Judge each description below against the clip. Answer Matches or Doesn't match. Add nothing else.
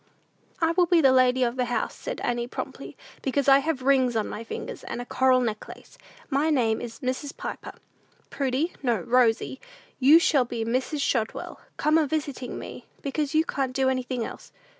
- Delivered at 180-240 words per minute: Matches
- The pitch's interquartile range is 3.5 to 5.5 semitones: Doesn't match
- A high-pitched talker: Matches